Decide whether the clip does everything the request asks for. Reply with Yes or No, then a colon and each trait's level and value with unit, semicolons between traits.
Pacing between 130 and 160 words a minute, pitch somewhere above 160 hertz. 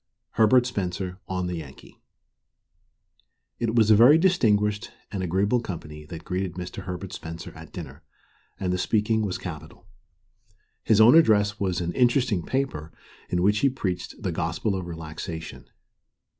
No: average, 145 wpm; very low, 95 Hz